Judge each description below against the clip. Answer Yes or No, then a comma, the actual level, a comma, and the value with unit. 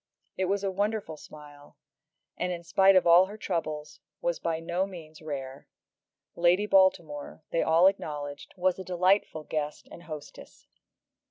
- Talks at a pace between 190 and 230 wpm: No, average, 150 wpm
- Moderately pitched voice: Yes, medium, 170 Hz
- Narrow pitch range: No, average, 3.6 semitones